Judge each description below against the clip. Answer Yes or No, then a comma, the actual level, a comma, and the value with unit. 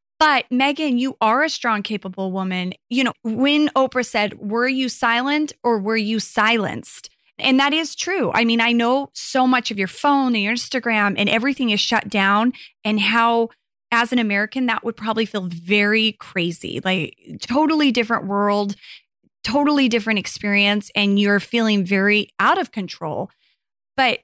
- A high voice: Yes, high, 225 Hz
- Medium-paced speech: Yes, average, 165 wpm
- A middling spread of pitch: Yes, average, 3.9 semitones